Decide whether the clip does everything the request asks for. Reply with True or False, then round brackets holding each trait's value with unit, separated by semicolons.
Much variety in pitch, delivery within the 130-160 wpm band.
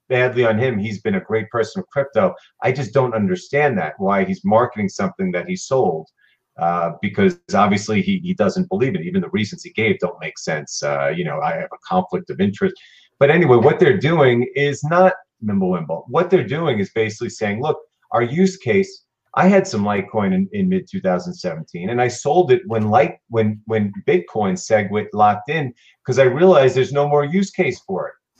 False (7.6 semitones; 200 wpm)